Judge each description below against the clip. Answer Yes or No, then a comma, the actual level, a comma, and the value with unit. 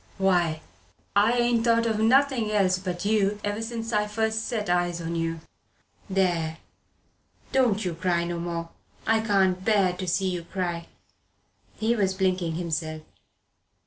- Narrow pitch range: No, average, 4.2 semitones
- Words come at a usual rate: Yes, average, 145 wpm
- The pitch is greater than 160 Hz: Yes, high, 190 Hz